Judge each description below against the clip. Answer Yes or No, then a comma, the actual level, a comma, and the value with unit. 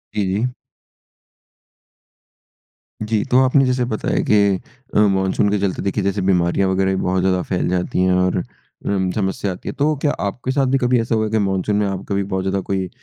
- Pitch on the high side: No, low, 100 Hz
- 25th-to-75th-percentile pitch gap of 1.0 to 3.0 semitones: Yes, narrow, 2.6 semitones